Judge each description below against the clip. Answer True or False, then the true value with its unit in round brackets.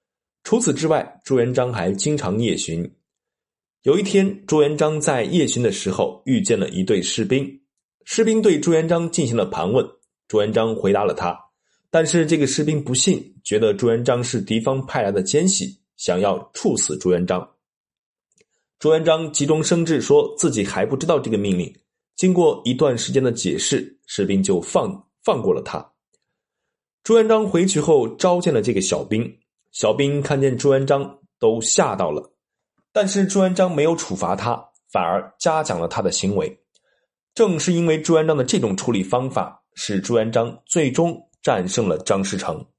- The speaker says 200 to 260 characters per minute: True (255 characters per minute)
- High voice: False (155 Hz)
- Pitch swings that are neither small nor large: False (6.3 semitones)